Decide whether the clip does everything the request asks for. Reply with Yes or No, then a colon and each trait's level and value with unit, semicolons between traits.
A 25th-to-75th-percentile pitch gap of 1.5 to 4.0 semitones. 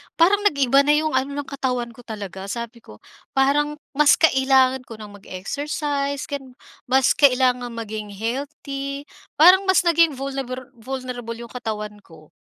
Yes: average, 3.5 semitones